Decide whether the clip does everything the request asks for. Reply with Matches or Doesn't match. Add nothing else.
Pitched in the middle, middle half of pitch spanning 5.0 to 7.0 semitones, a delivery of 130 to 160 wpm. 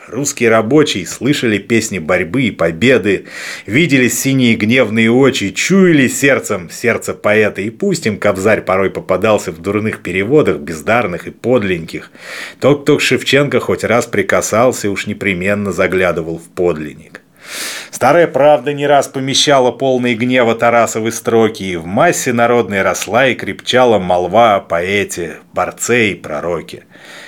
Doesn't match